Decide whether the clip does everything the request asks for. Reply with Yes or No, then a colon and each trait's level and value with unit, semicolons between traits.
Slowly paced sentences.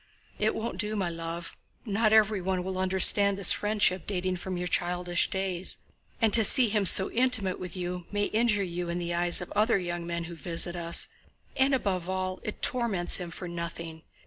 No: average, 190 wpm